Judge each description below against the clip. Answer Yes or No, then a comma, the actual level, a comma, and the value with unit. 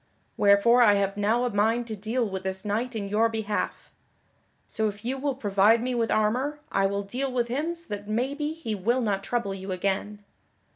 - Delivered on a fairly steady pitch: No, average, 3.4 semitones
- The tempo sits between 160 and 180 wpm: No, average, 200 wpm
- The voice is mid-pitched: No, high, 220 Hz